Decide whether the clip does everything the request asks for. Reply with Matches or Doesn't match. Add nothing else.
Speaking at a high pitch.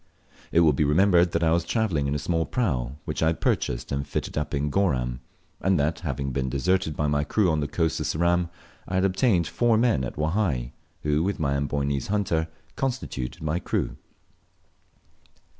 Doesn't match